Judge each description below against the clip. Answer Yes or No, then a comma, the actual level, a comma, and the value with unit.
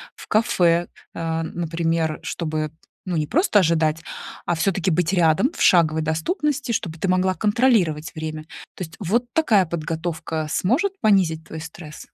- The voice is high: No, medium, 170 Hz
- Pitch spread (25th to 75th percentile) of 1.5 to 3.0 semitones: No, average, 3.6 semitones